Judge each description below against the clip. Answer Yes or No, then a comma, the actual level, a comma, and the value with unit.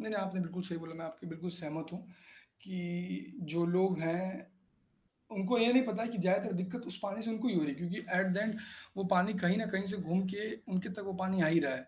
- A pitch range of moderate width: Yes, average, 3.1 semitones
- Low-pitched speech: No, medium, 185 Hz